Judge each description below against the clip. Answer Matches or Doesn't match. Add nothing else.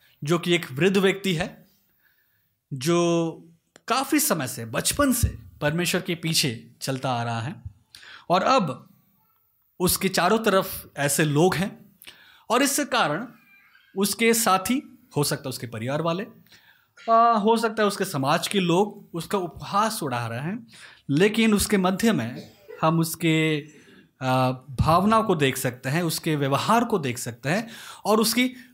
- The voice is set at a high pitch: Doesn't match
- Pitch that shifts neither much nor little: Doesn't match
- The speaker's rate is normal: Matches